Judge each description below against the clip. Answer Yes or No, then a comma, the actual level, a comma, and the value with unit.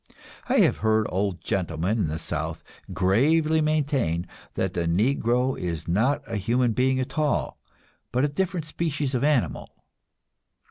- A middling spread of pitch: No, wide, 7.4 semitones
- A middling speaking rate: Yes, average, 145 wpm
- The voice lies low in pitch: Yes, low, 125 Hz